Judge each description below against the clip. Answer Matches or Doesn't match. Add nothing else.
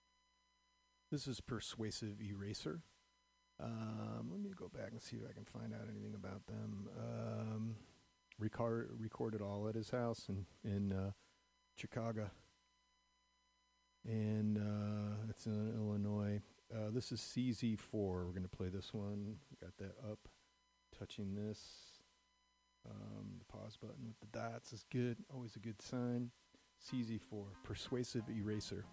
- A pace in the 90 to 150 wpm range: Matches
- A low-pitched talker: Matches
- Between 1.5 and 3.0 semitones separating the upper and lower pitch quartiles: Matches